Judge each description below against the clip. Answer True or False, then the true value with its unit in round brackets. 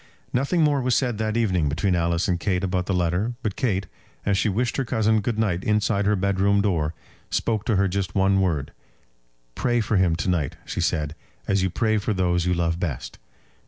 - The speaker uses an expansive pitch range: False (3.6 semitones)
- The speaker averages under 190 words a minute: False (205 wpm)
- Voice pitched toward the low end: True (100 Hz)